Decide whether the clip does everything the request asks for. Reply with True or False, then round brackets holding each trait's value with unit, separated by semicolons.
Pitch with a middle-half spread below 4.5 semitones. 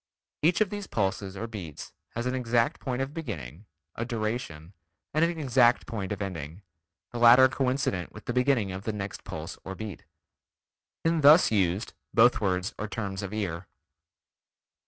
False (5.2 semitones)